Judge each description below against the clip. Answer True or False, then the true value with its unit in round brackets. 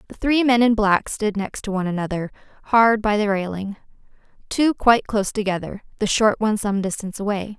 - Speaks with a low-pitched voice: False (210 Hz)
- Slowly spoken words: False (190 wpm)